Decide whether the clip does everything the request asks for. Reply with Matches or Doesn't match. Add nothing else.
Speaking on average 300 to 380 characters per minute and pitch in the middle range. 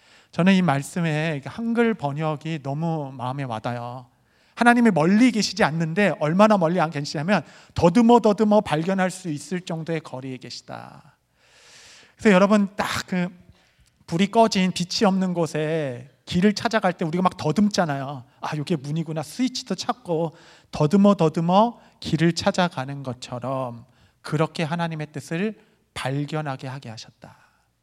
Matches